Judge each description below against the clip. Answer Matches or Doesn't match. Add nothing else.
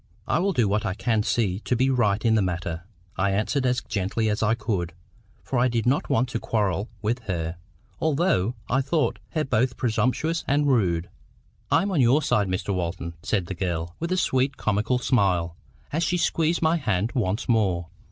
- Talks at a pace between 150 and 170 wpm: Doesn't match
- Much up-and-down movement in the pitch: Matches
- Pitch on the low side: Matches